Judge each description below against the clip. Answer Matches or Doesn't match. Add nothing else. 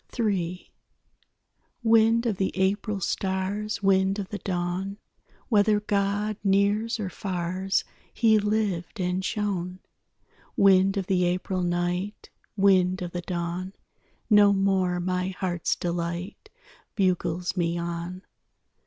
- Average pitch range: Doesn't match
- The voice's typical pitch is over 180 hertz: Matches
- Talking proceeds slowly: Matches